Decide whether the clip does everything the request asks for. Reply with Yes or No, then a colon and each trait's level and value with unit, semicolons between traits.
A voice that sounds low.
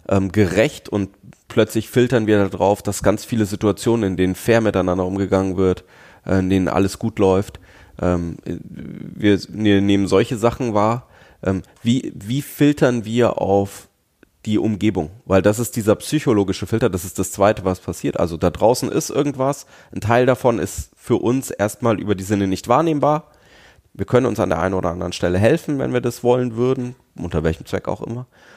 Yes: low, 105 Hz